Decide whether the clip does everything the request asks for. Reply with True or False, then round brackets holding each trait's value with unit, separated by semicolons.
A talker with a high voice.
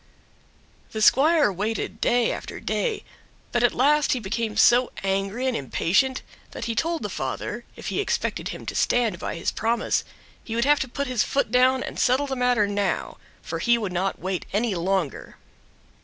True (235 Hz)